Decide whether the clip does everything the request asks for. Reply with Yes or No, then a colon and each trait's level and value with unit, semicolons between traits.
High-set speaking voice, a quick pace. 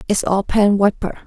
No: high, 200 Hz; average, 190 wpm